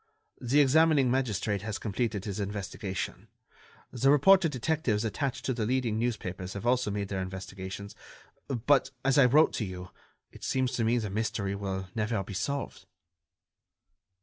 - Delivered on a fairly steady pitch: No, average, 4.7 semitones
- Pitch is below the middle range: Yes, low, 110 Hz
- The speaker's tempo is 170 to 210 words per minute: No, average, 150 wpm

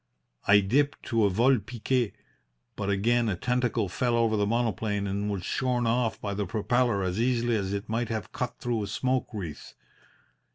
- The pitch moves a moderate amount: Yes, average, 3.2 semitones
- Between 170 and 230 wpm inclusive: Yes, average, 180 wpm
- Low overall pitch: Yes, low, 115 Hz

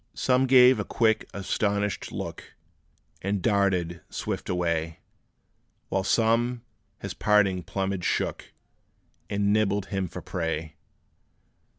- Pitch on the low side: Yes, low, 100 Hz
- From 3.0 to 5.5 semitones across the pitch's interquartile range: Yes, average, 3.3 semitones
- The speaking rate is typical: No, slow, 105 wpm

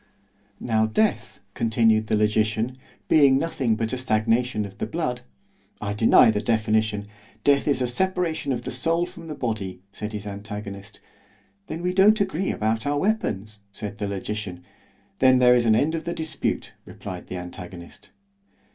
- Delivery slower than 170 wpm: Yes, average, 155 wpm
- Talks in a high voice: No, low, 110 Hz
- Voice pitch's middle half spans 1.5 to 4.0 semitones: No, average, 5.1 semitones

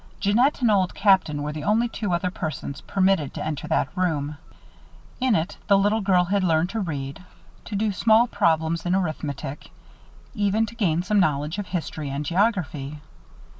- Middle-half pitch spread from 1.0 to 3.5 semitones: No, average, 5.0 semitones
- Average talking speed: Yes, average, 170 wpm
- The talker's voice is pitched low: No, medium, 180 Hz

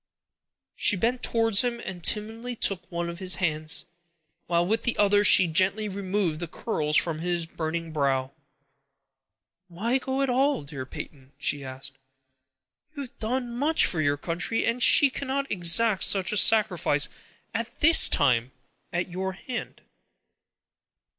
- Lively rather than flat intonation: Yes, wide, 5.9 semitones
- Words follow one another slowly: No, average, 145 wpm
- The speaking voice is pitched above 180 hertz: Yes, high, 190 Hz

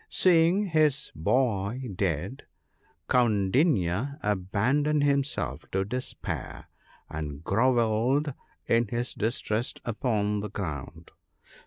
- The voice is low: Yes, low, 115 Hz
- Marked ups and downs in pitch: Yes, wide, 5.9 semitones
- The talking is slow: Yes, slow, 85 wpm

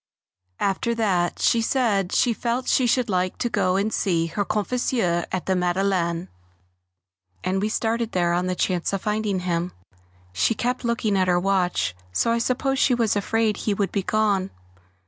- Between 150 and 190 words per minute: Yes, average, 175 wpm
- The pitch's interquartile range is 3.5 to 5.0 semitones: Yes, average, 4.0 semitones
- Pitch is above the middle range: Yes, high, 200 Hz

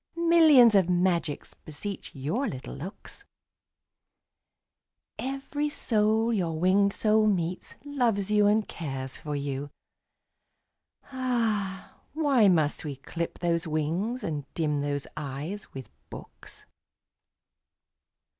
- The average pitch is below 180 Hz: No, high, 190 Hz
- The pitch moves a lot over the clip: Yes, wide, 6.7 semitones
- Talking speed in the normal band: No, slow, 105 wpm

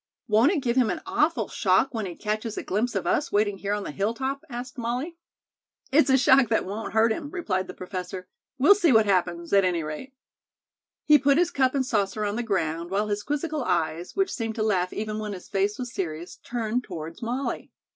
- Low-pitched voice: No, high, 220 Hz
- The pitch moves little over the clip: No, wide, 5.5 semitones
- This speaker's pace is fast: Yes, fast, 215 wpm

